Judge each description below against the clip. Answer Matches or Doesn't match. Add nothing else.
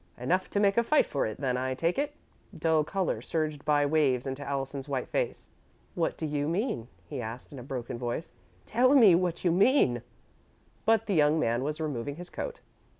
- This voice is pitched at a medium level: Matches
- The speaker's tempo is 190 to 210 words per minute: Matches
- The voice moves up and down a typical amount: Doesn't match